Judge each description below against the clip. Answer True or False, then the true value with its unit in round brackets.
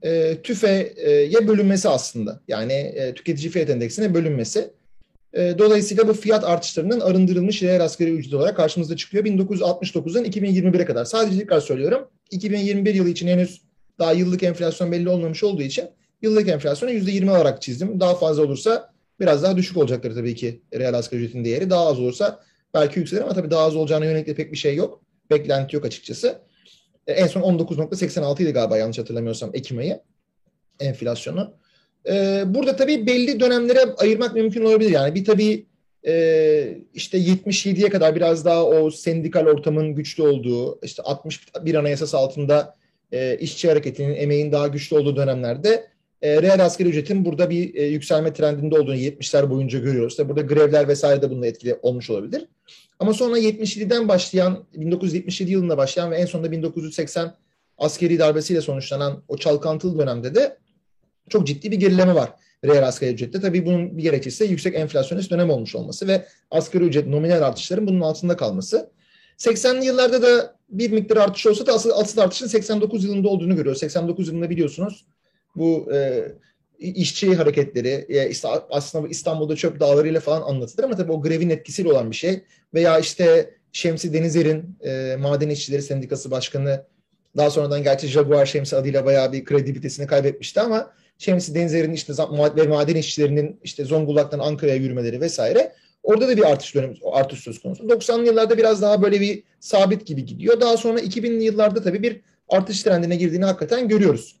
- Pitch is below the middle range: False (170 Hz)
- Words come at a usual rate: False (160 wpm)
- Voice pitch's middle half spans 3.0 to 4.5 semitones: False (5.3 semitones)